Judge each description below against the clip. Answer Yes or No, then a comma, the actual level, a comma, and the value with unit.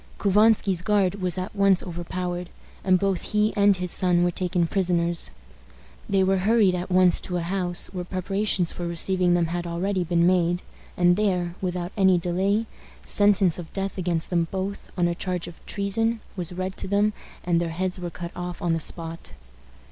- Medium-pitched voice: Yes, medium, 180 Hz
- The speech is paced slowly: No, average, 185 wpm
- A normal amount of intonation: No, narrow, 2.0 semitones